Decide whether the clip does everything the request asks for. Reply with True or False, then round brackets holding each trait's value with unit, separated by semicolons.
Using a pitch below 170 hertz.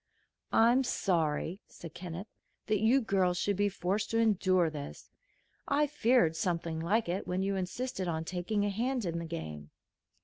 False (190 Hz)